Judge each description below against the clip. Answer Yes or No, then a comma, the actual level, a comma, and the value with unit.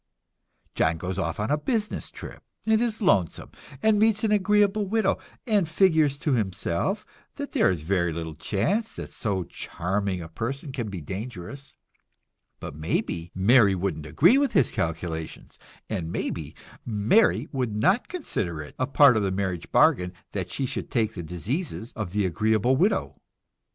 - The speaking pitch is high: No, low, 110 Hz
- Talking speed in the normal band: Yes, average, 160 wpm